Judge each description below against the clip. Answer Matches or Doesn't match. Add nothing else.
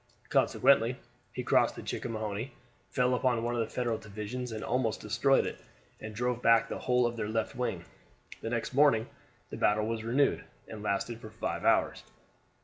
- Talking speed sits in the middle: Matches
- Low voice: Matches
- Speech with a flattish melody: Matches